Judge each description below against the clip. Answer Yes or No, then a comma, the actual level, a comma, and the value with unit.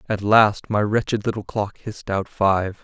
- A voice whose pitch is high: No, low, 105 Hz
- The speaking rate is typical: Yes, average, 190 wpm